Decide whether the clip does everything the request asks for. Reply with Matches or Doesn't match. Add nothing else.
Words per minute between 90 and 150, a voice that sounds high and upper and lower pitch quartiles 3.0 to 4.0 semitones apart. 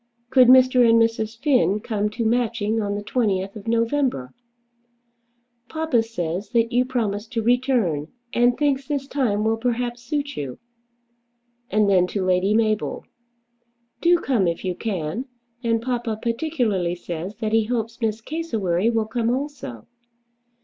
Matches